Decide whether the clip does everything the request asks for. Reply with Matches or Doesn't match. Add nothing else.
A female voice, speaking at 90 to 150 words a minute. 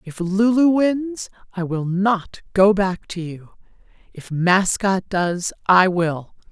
Matches